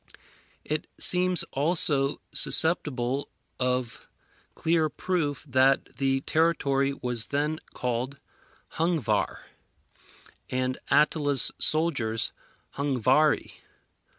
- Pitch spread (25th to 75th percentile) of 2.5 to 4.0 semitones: Yes, average, 3.5 semitones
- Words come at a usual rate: No, slow, 75 wpm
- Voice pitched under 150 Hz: Yes, medium, 140 Hz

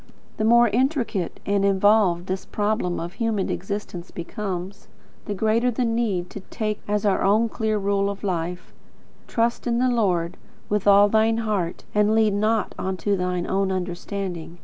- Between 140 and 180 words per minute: Yes, average, 160 wpm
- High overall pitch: Yes, high, 200 Hz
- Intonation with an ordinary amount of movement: Yes, average, 3.0 semitones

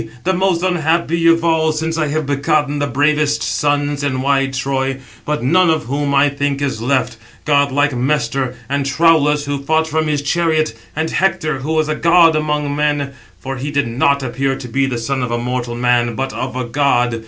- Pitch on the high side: No, medium, 145 Hz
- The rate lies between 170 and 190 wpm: No, average, 200 wpm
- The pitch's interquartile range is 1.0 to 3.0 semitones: Yes, average, 2.7 semitones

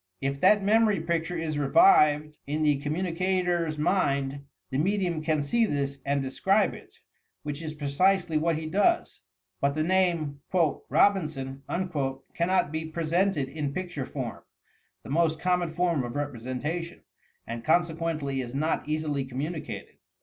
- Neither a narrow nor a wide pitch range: Yes, average, 3.9 semitones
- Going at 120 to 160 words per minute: Yes, average, 145 wpm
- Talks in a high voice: No, medium, 155 Hz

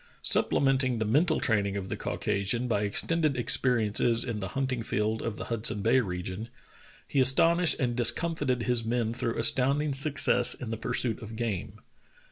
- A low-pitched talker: Yes, low, 120 Hz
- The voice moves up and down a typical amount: Yes, average, 3.5 semitones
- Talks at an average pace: Yes, average, 165 wpm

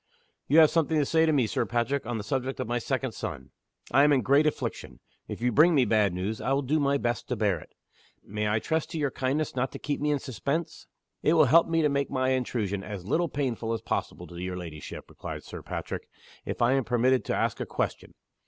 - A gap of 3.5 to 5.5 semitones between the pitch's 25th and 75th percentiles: Yes, average, 4.7 semitones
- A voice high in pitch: No, low, 130 Hz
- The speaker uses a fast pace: Yes, fast, 240 wpm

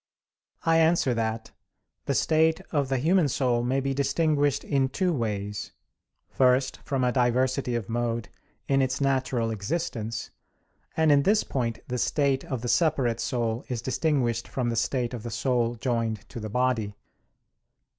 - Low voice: Yes, low, 125 Hz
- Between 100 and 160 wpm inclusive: Yes, average, 155 wpm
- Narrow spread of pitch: No, average, 3.2 semitones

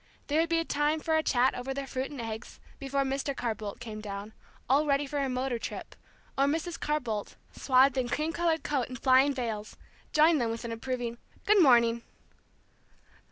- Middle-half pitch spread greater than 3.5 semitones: Yes, average, 3.9 semitones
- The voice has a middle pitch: No, very high, 265 Hz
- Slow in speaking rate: No, average, 195 wpm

